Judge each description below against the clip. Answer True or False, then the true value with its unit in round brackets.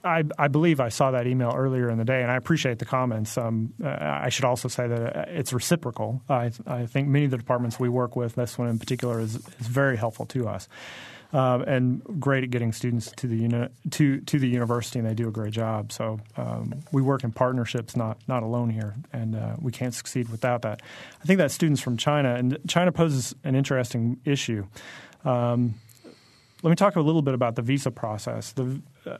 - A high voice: False (125 Hz)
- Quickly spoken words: True (215 wpm)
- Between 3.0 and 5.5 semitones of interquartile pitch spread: False (2.6 semitones)